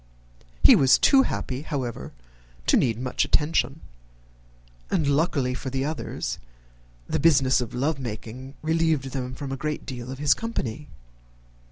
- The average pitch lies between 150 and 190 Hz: No, low, 135 Hz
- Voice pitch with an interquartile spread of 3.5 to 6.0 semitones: No, average, 3.1 semitones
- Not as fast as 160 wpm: Yes, average, 145 wpm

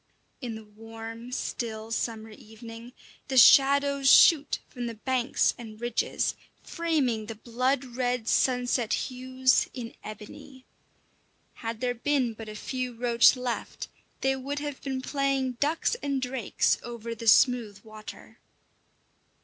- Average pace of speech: No, slow, 130 wpm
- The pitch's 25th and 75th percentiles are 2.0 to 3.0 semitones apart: Yes, average, 2.7 semitones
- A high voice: Yes, high, 245 Hz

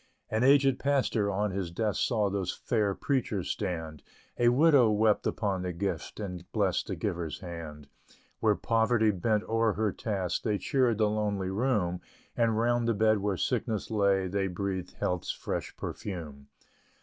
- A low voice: Yes, low, 105 Hz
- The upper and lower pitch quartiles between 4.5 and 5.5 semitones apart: No, average, 3.4 semitones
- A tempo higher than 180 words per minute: No, average, 160 wpm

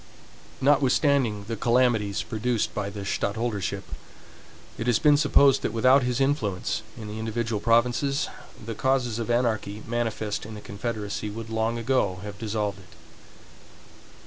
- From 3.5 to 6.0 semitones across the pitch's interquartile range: No, average, 3.0 semitones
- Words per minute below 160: Yes, average, 140 wpm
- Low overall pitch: Yes, low, 115 Hz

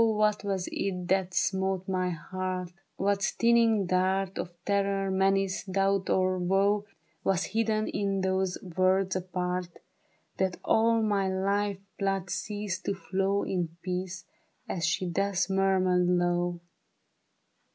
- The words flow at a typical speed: No, slow, 125 wpm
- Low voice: No, high, 190 Hz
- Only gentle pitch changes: Yes, narrow, 1.4 semitones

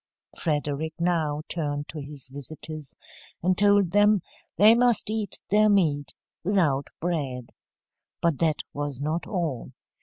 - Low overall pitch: No, medium, 160 Hz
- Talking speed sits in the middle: No, slow, 125 wpm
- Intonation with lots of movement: No, average, 5.0 semitones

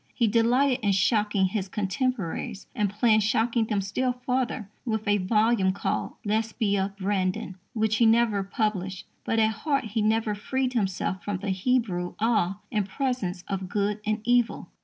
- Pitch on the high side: Yes, high, 215 Hz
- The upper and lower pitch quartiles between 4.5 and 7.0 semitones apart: No, average, 3.0 semitones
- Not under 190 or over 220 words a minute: No, average, 160 wpm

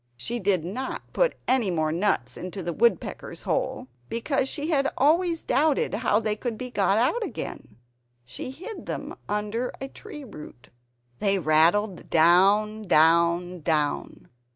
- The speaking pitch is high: Yes, high, 210 Hz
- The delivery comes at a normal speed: Yes, average, 145 wpm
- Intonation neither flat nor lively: No, wide, 7.1 semitones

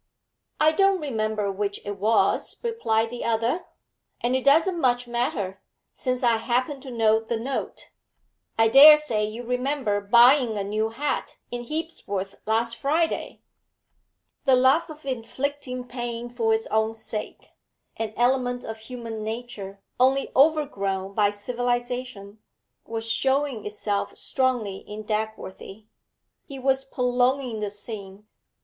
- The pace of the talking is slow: Yes, slow, 130 wpm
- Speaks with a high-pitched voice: Yes, high, 240 Hz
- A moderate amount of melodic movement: Yes, average, 3.4 semitones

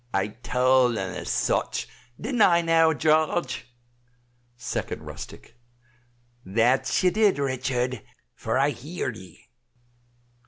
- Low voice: Yes, low, 130 Hz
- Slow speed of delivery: Yes, slow, 110 wpm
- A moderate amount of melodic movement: Yes, average, 5.0 semitones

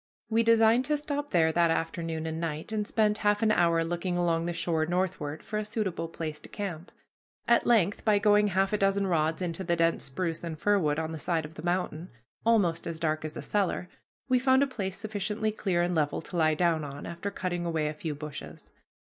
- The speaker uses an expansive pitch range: No, average, 4.2 semitones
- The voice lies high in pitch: No, medium, 175 Hz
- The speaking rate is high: Yes, fast, 220 wpm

